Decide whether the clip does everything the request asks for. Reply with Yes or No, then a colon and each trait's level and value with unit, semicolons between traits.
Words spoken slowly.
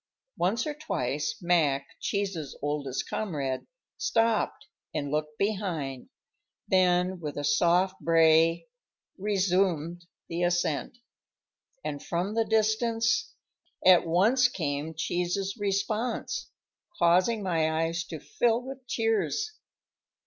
Yes: slow, 105 wpm